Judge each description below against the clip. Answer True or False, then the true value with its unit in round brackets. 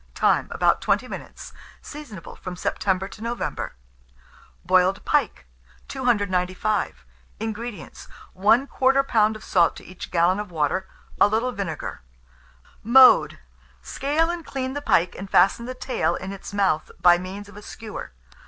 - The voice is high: True (205 Hz)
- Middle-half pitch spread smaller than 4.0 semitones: False (4.9 semitones)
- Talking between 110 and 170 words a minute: True (140 wpm)